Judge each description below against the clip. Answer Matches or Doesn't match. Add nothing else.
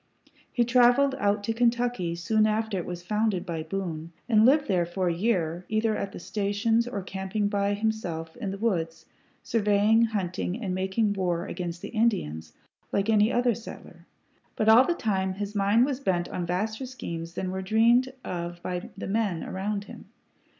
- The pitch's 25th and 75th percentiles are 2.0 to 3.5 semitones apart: Doesn't match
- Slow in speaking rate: Doesn't match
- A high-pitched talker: Matches